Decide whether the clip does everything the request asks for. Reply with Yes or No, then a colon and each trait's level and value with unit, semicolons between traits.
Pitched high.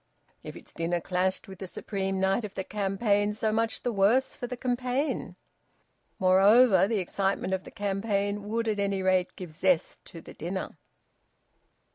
Yes: high, 195 Hz